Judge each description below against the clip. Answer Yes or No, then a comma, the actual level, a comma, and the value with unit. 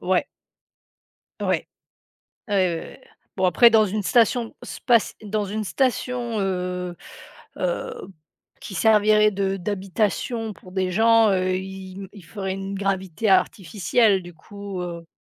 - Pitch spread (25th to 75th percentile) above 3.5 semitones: No, average, 2.7 semitones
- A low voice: No, high, 195 Hz